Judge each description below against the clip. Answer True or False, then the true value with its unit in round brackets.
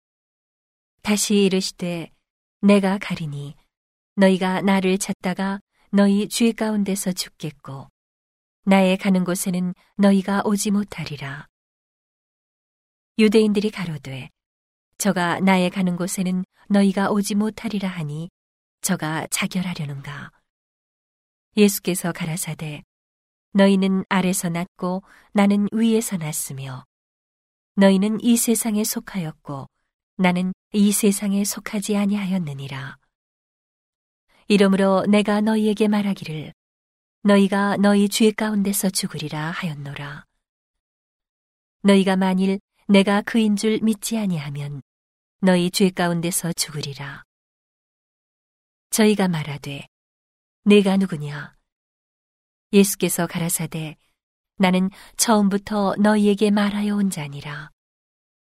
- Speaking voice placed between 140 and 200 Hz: True (190 Hz)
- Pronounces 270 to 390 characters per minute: False (235 characters per minute)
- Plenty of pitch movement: False (4.5 semitones)